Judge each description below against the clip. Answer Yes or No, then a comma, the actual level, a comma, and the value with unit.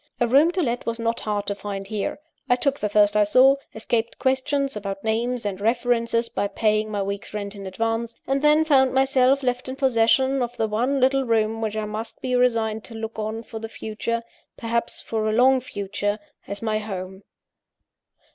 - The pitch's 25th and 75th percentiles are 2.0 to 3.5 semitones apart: Yes, average, 3.0 semitones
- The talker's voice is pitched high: Yes, high, 230 Hz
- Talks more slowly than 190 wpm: No, average, 195 wpm